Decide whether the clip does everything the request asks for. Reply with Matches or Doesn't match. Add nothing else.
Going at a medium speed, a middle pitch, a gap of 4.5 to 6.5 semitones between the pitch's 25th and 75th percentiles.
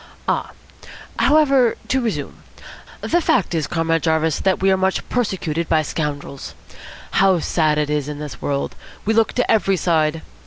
Matches